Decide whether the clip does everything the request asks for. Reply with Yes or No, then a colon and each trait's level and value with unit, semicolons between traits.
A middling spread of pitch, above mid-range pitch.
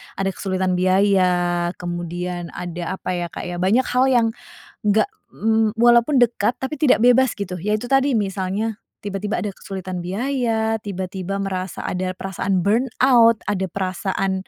Yes: average, 3.6 semitones; high, 195 Hz